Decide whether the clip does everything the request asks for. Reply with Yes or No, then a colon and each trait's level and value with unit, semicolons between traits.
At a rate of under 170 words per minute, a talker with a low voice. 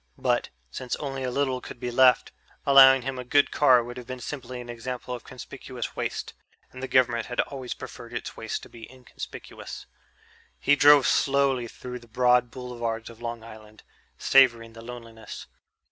No: average, 175 wpm; low, 125 Hz